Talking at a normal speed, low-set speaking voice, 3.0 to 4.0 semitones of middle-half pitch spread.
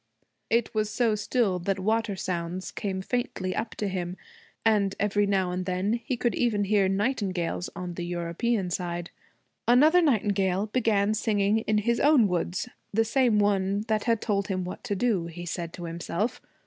No: average, 175 wpm; high, 200 Hz; average, 3.4 semitones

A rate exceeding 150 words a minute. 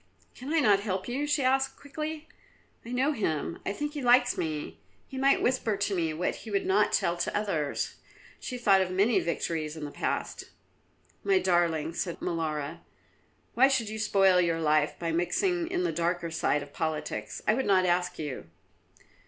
Yes: average, 185 wpm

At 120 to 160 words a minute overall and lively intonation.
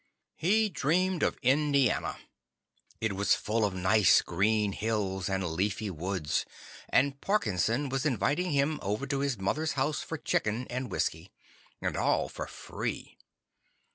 Yes: average, 140 wpm; wide, 6.6 semitones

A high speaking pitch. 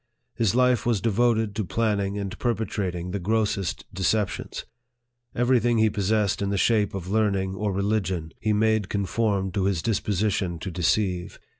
No: low, 100 Hz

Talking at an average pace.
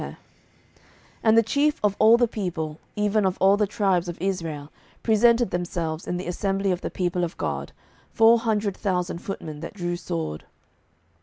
Yes: average, 170 wpm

